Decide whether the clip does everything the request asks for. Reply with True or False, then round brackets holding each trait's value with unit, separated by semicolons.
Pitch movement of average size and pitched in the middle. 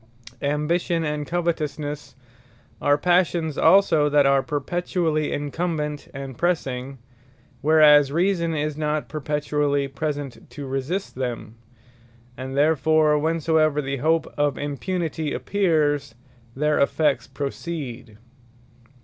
False (2.3 semitones; 150 Hz)